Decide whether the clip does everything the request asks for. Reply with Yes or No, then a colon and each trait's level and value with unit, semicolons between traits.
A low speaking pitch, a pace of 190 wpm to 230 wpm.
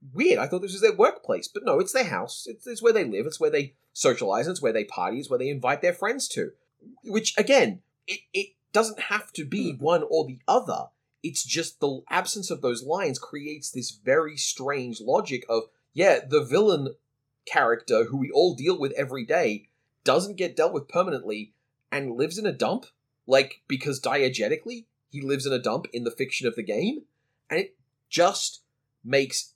No: medium, 165 Hz; average, 195 wpm